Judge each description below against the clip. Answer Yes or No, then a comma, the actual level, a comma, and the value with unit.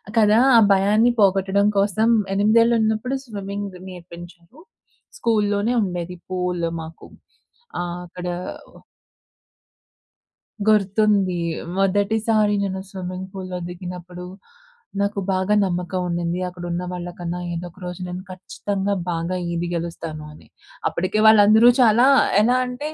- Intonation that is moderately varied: Yes, average, 3.0 semitones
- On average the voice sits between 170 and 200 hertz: Yes, high, 190 Hz